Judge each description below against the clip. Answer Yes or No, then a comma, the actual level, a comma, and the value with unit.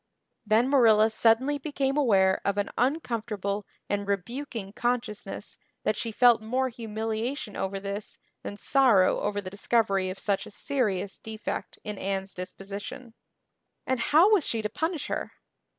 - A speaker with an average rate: Yes, average, 145 wpm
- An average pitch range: Yes, average, 4.0 semitones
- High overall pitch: Yes, high, 220 Hz